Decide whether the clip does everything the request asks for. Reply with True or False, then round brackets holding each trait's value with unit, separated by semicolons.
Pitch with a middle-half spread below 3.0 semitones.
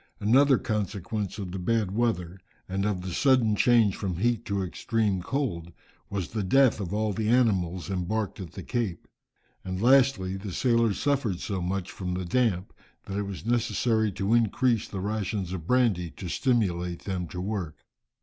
False (3.9 semitones)